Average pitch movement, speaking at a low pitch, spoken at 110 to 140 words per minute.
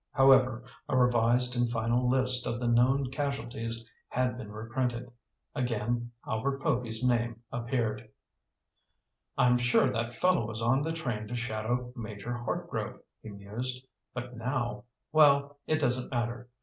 No: narrow, 1.7 semitones; low, 120 Hz; slow, 135 wpm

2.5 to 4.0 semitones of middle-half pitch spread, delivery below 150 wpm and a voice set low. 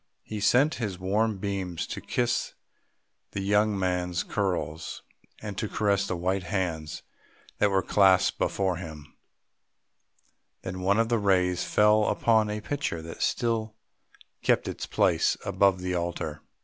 Yes: average, 2.9 semitones; average, 140 wpm; very low, 95 Hz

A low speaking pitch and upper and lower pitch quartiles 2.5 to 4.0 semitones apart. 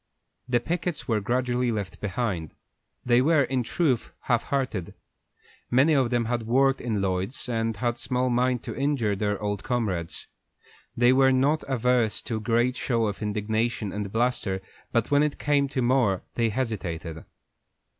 Yes: low, 120 Hz; average, 3.5 semitones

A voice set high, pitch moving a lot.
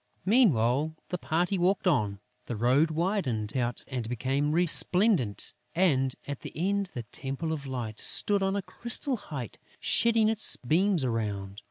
No: medium, 150 Hz; wide, 7.9 semitones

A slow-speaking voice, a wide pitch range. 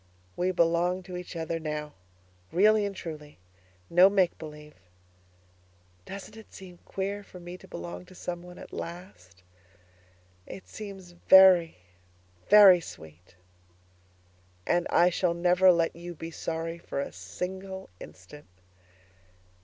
No: slow, 125 wpm; average, 2.7 semitones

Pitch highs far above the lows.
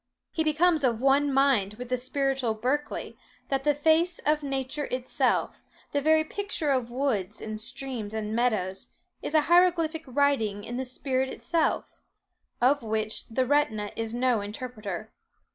No: average, 4.7 semitones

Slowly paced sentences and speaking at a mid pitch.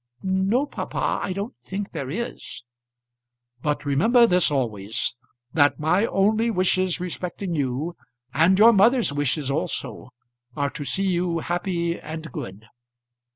Yes: slow, 130 wpm; medium, 175 Hz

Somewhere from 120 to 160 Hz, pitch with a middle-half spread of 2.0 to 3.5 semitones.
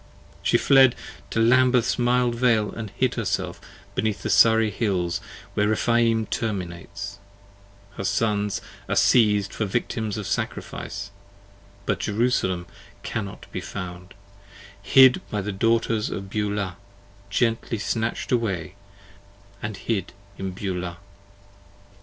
No: low, 105 Hz; average, 2.9 semitones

